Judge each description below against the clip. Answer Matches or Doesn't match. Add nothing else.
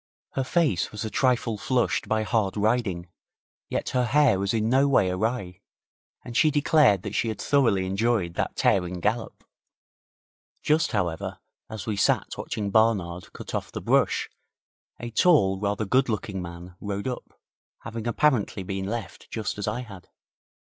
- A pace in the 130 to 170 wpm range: Matches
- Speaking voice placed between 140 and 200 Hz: Doesn't match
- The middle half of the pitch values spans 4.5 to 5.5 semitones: Doesn't match